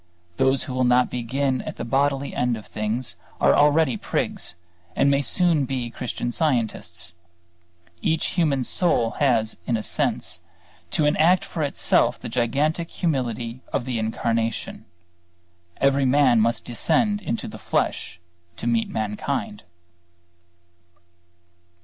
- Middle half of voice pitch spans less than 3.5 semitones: No, average, 3.8 semitones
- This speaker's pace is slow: Yes, slow, 130 wpm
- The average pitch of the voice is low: Yes, low, 125 Hz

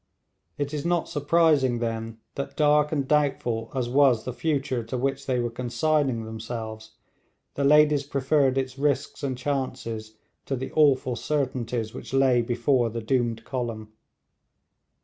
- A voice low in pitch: Yes, low, 130 Hz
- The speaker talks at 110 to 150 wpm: Yes, average, 145 wpm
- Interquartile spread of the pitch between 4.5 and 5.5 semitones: No, average, 3.4 semitones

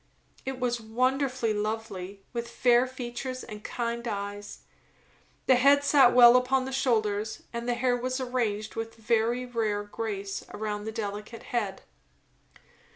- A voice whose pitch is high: Yes, high, 235 Hz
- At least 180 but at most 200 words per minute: No, average, 140 wpm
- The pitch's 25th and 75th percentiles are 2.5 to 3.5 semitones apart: Yes, average, 2.9 semitones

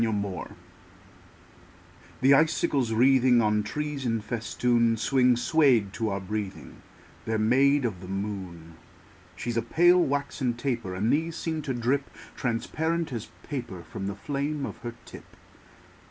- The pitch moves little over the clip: No, average, 4.8 semitones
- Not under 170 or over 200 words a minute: No, average, 140 wpm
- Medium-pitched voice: No, low, 120 Hz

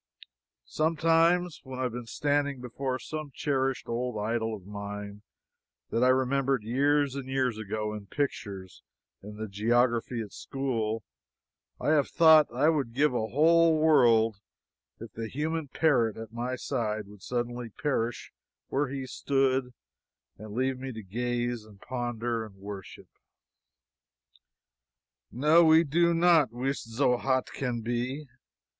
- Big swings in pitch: No, average, 4.1 semitones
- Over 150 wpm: No, average, 140 wpm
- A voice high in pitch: No, low, 125 Hz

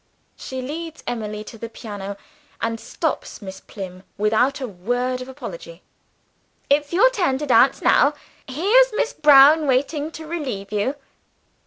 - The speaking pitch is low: No, very high, 260 Hz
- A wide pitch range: Yes, wide, 5.9 semitones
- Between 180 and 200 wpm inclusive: No, average, 145 wpm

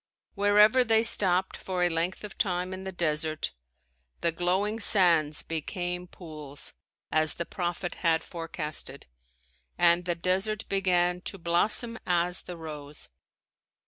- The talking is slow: Yes, slow, 130 wpm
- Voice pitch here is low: No, medium, 175 Hz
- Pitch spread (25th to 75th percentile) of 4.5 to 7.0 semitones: No, narrow, 2.6 semitones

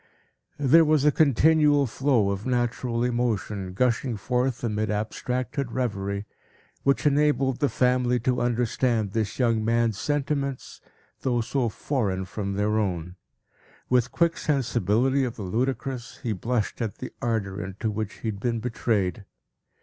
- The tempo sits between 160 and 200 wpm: No, average, 140 wpm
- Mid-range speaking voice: No, low, 120 Hz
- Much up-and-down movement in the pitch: No, average, 3.7 semitones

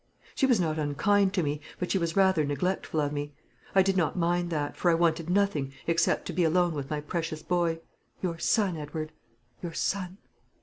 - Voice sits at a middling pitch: Yes, medium, 170 Hz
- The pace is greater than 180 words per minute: Yes, average, 200 wpm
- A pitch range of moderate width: Yes, average, 3.0 semitones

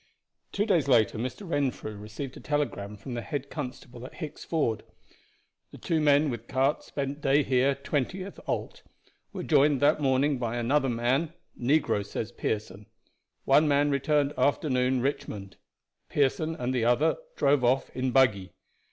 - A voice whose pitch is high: No, low, 135 Hz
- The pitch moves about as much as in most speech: Yes, average, 3.4 semitones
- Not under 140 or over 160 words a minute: Yes, average, 150 wpm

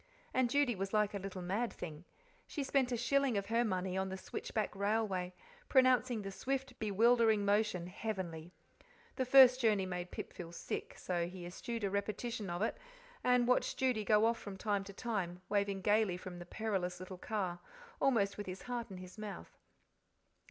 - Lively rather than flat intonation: No, average, 4.0 semitones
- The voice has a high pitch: Yes, high, 205 Hz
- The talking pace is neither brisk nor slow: Yes, average, 180 wpm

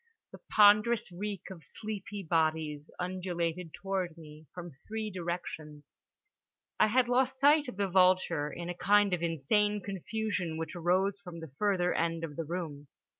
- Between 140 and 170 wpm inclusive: Yes, average, 155 wpm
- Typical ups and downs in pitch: Yes, average, 3.9 semitones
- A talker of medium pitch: Yes, medium, 180 Hz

